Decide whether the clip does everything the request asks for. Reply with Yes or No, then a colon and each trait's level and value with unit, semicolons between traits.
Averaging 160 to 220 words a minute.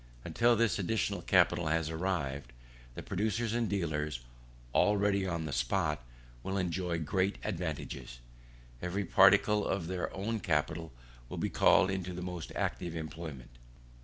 No: slow, 135 wpm